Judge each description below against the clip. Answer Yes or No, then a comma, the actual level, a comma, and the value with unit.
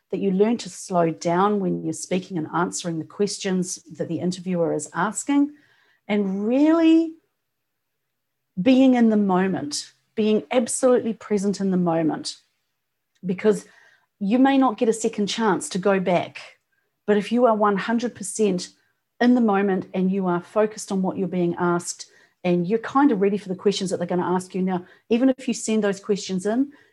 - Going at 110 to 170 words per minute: No, average, 180 wpm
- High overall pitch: Yes, high, 200 Hz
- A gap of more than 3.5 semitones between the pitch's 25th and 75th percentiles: Yes, average, 4.0 semitones